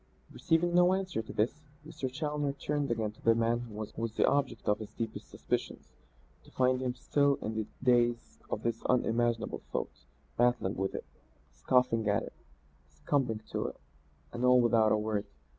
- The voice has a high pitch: No, low, 120 Hz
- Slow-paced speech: No, average, 175 wpm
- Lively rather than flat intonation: No, average, 3.5 semitones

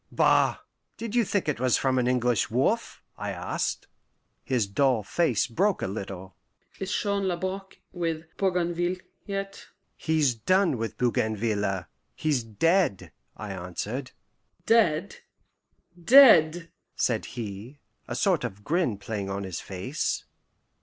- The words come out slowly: Yes, slow, 125 wpm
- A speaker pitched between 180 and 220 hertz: No, low, 135 Hz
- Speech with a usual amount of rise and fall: No, wide, 8.9 semitones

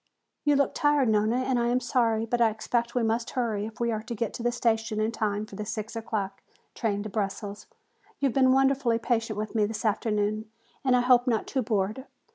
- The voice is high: Yes, high, 225 Hz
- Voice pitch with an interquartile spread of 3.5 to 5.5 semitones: No, narrow, 2.4 semitones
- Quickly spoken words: Yes, fast, 225 wpm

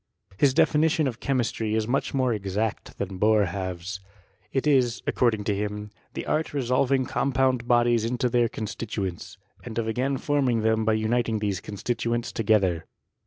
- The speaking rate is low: No, average, 155 wpm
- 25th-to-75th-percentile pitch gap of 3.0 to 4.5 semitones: Yes, average, 3.4 semitones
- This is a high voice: No, low, 115 Hz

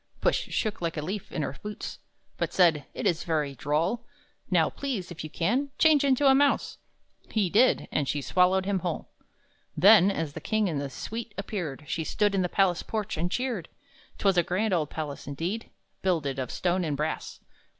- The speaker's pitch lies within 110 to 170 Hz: No, medium, 180 Hz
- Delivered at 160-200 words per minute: Yes, average, 190 wpm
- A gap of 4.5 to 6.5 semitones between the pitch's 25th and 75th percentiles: Yes, average, 5.2 semitones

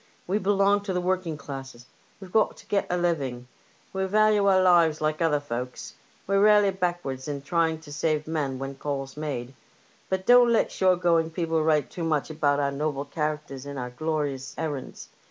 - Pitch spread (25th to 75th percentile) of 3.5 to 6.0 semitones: Yes, average, 4.6 semitones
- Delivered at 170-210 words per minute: Yes, average, 190 wpm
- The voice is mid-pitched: Yes, medium, 155 Hz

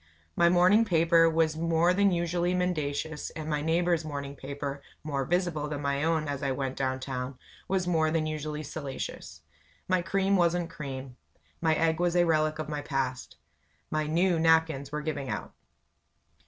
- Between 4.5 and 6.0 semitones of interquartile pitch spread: No, average, 3.3 semitones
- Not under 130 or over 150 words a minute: No, average, 165 wpm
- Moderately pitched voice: Yes, medium, 155 Hz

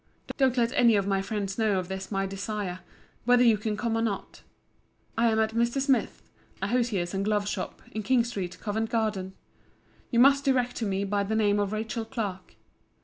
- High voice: Yes, high, 215 Hz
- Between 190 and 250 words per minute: Yes, average, 200 wpm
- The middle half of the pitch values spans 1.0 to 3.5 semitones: Yes, average, 3.1 semitones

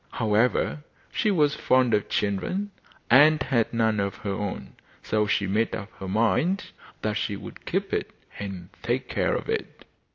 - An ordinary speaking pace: Yes, average, 165 wpm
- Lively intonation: No, average, 4.4 semitones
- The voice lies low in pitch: Yes, low, 110 Hz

